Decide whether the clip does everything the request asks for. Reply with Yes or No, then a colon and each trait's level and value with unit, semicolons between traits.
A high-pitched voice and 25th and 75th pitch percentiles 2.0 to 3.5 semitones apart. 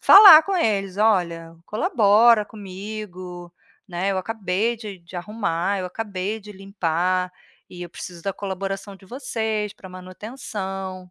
Yes: high, 195 Hz; average, 2.8 semitones